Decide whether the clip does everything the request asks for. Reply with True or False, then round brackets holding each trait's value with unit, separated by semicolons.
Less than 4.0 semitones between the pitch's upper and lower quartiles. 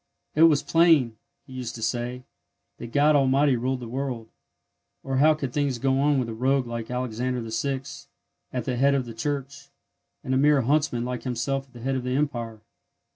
True (2.6 semitones)